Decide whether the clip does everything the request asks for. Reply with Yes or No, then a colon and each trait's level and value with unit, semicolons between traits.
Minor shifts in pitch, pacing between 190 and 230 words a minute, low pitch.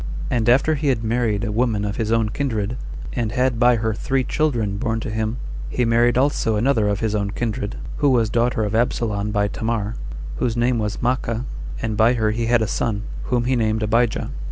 Yes: narrow, 2.2 semitones; fast, 205 wpm; low, 115 Hz